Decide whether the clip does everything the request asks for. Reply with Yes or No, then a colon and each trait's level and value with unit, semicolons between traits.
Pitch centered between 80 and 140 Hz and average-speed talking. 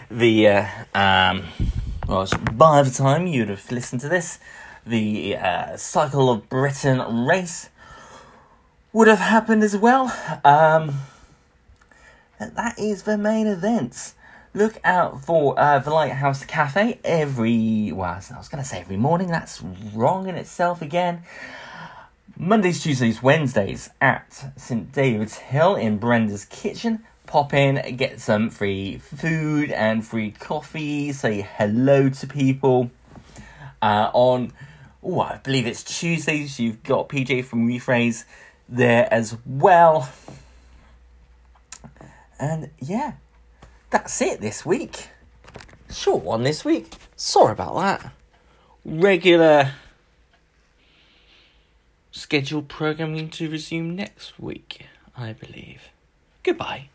No: low, 135 Hz; slow, 120 wpm